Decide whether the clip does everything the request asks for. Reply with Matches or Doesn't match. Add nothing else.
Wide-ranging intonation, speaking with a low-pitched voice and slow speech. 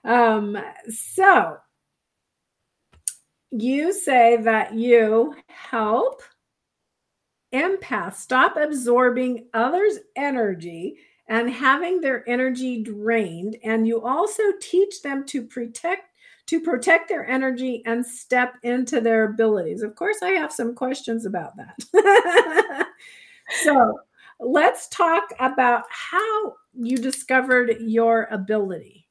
Doesn't match